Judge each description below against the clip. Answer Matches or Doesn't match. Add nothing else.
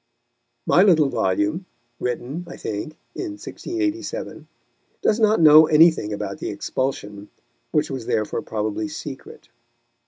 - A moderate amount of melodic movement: Doesn't match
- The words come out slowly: Matches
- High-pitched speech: Doesn't match